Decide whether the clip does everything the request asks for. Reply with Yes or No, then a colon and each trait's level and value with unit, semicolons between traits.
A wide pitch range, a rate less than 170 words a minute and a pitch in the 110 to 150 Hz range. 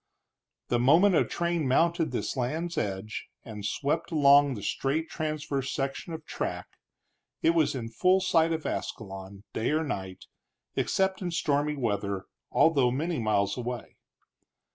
Yes: wide, 6.2 semitones; average, 140 wpm; medium, 140 Hz